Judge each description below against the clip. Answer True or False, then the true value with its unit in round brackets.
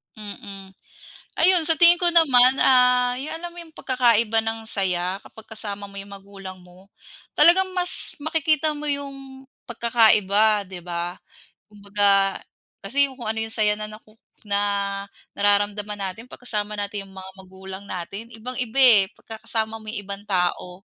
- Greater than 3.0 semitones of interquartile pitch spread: True (4.2 semitones)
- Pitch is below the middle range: False (215 Hz)